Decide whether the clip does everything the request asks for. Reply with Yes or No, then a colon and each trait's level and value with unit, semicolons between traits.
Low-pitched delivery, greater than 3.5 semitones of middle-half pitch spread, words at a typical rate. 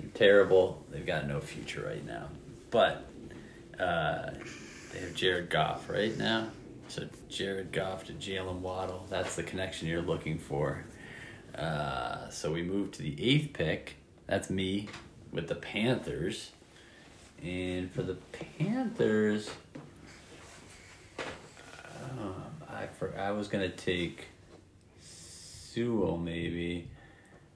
No: very low, 95 Hz; average, 3.9 semitones; slow, 120 wpm